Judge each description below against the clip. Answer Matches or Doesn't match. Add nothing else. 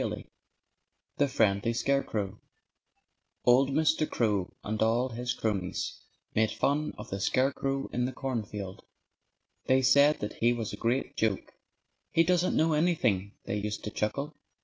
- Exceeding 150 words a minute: Doesn't match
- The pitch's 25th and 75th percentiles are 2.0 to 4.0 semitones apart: Doesn't match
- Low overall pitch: Matches